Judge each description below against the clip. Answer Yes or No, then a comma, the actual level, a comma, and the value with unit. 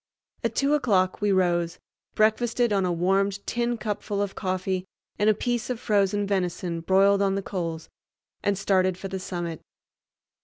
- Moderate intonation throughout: No, narrow, 2.1 semitones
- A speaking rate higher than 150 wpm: Yes, average, 160 wpm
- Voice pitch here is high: Yes, high, 195 Hz